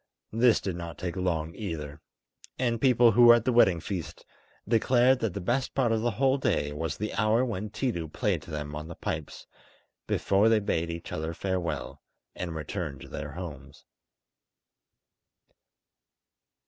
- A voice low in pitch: Yes, very low, 95 Hz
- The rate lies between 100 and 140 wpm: No, average, 160 wpm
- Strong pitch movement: Yes, wide, 6.1 semitones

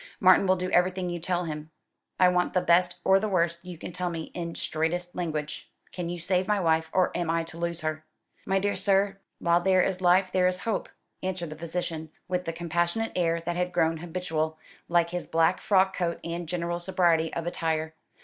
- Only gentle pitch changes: Yes, narrow, 1.8 semitones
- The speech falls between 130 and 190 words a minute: No, fast, 205 wpm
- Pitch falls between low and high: Yes, medium, 175 Hz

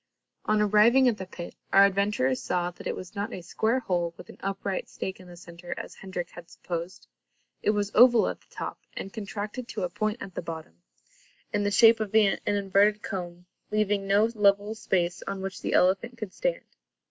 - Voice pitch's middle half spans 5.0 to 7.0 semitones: No, average, 3.0 semitones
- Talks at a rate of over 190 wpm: Yes, average, 200 wpm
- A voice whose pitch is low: No, high, 200 Hz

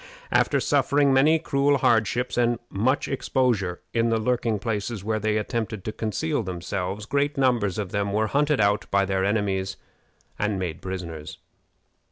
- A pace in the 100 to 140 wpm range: No, average, 155 wpm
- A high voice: No, low, 110 Hz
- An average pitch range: Yes, average, 4.2 semitones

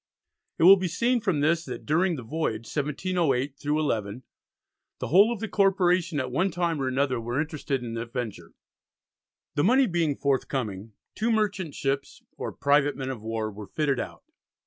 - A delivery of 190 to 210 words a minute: No, average, 170 wpm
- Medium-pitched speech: Yes, medium, 145 Hz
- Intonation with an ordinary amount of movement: No, wide, 5.8 semitones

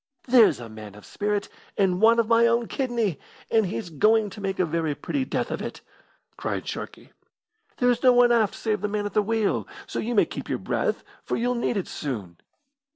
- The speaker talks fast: Yes, fast, 210 wpm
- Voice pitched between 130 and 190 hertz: No, high, 210 Hz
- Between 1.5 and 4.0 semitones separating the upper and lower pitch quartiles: No, average, 4.6 semitones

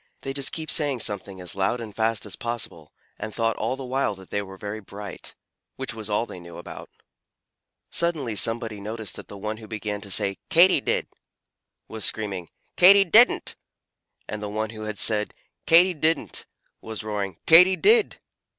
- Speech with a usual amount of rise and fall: Yes, average, 4.8 semitones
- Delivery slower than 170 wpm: No, average, 180 wpm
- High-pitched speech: No, low, 110 Hz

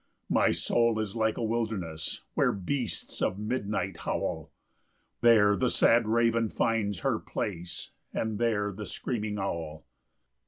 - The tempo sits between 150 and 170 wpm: No, average, 140 wpm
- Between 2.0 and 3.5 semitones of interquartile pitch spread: Yes, narrow, 2.6 semitones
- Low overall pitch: Yes, low, 110 Hz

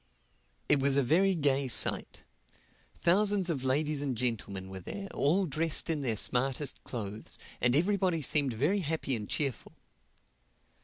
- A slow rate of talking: No, average, 145 wpm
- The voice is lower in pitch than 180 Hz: Yes, medium, 140 Hz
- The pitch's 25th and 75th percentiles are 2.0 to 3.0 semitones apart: No, average, 5.0 semitones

